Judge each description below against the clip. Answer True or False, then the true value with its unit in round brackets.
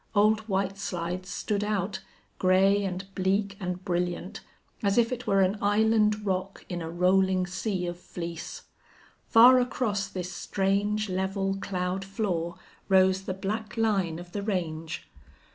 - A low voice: False (195 Hz)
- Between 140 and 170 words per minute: True (145 wpm)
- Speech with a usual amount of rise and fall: False (2.3 semitones)